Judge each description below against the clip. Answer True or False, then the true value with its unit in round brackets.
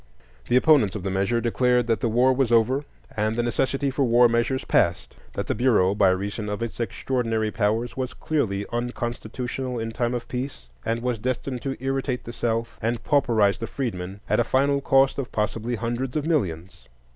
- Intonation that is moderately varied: True (3.0 semitones)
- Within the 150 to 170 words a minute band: False (190 wpm)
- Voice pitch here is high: False (120 Hz)